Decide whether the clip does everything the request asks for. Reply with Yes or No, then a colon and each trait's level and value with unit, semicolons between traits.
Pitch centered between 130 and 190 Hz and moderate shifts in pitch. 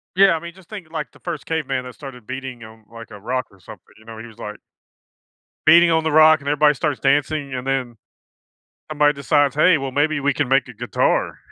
Yes: medium, 140 Hz; average, 3.8 semitones